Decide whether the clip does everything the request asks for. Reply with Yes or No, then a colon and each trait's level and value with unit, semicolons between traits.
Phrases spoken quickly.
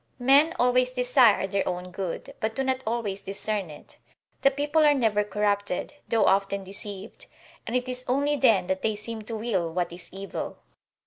No: average, 180 wpm